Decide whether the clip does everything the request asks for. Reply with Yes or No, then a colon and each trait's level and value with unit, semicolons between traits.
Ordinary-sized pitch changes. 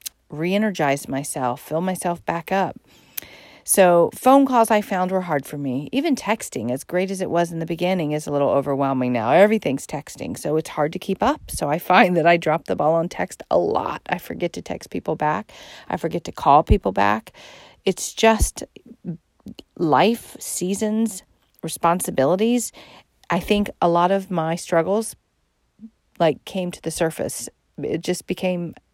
Yes: average, 4.0 semitones